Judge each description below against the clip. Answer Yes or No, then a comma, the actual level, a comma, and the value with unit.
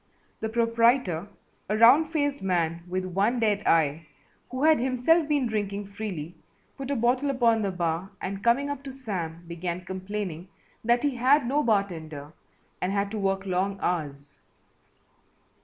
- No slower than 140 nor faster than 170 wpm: Yes, average, 155 wpm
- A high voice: Yes, high, 205 Hz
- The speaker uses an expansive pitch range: Yes, wide, 5.8 semitones